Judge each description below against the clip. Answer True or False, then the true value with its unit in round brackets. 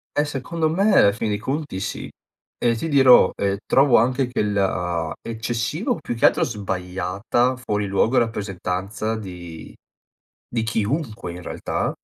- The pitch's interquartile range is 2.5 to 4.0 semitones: False (4.9 semitones)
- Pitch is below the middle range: True (110 Hz)